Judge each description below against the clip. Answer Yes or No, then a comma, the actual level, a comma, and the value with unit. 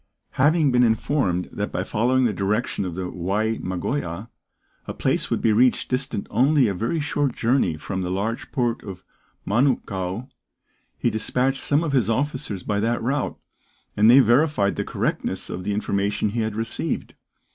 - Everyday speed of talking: Yes, average, 170 wpm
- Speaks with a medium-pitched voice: No, low, 115 Hz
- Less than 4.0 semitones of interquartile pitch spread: No, average, 4.6 semitones